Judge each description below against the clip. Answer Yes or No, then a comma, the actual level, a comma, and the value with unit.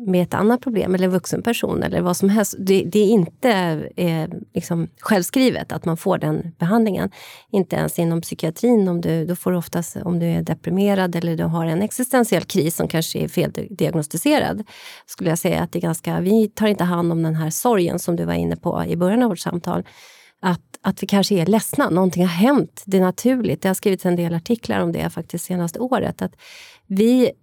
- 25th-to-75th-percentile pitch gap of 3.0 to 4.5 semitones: Yes, average, 4.1 semitones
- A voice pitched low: No, medium, 185 Hz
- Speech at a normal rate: No, fast, 215 wpm